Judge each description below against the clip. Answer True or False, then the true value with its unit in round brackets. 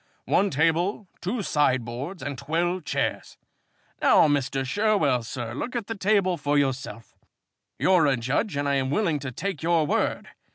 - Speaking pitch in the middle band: True (150 Hz)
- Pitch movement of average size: False (6.0 semitones)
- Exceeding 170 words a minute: False (160 wpm)